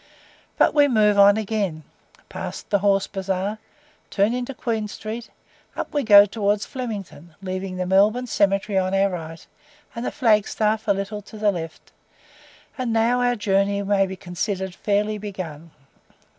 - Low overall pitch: No, high, 205 Hz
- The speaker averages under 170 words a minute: Yes, average, 155 wpm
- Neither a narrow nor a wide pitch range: No, narrow, 2.3 semitones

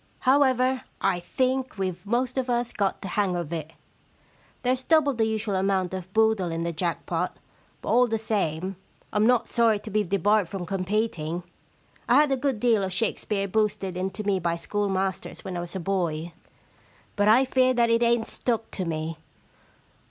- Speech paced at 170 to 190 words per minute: Yes, average, 180 wpm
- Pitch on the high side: Yes, high, 205 Hz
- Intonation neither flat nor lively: Yes, average, 4.4 semitones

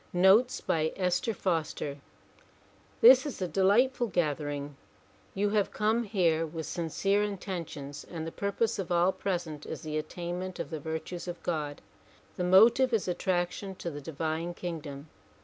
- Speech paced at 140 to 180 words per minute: Yes, average, 150 wpm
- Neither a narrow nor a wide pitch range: Yes, average, 3.9 semitones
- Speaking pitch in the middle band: Yes, medium, 175 Hz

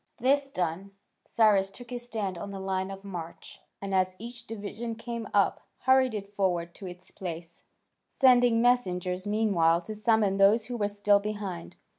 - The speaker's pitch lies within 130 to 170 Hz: No, high, 205 Hz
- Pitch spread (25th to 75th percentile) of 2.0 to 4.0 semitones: Yes, average, 3.5 semitones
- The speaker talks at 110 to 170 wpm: Yes, average, 165 wpm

